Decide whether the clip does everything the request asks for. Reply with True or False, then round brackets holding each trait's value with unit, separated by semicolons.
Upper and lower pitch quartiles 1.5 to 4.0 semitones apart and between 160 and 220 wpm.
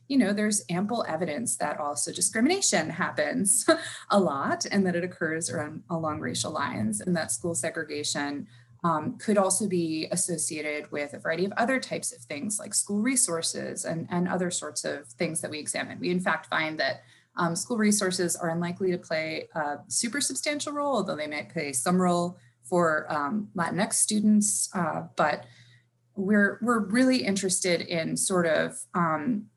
False (4.8 semitones; 170 wpm)